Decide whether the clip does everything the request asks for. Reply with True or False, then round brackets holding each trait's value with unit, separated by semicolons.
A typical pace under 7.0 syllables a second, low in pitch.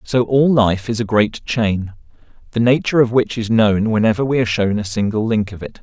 True (5.5 syllables/s; 110 Hz)